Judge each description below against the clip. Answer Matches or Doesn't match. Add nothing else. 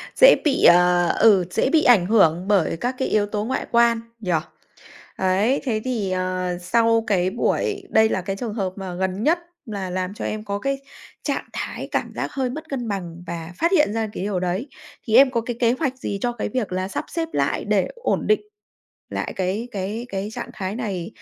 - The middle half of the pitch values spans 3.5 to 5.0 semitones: Matches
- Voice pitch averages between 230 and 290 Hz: Doesn't match